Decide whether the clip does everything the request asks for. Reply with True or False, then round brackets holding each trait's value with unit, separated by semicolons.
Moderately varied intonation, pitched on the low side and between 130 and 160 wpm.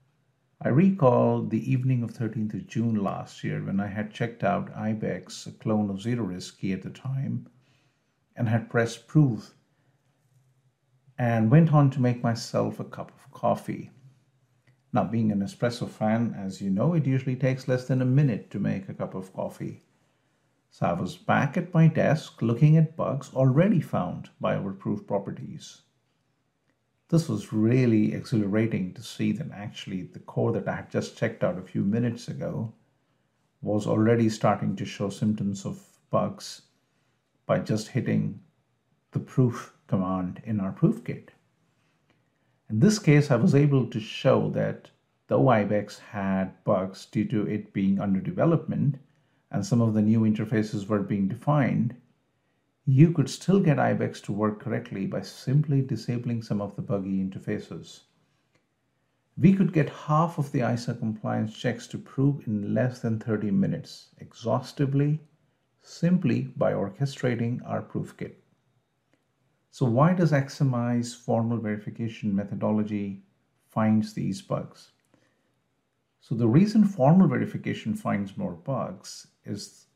True (4.4 semitones; 125 Hz; 150 wpm)